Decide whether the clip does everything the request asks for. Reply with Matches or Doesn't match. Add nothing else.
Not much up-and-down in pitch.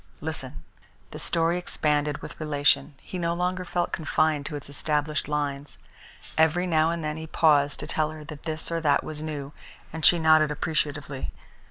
Matches